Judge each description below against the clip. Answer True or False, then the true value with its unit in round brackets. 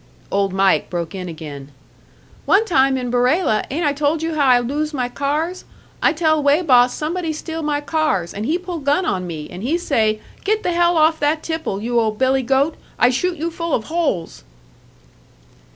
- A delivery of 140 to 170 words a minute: False (195 wpm)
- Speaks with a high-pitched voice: True (285 Hz)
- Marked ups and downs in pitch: True (5.7 semitones)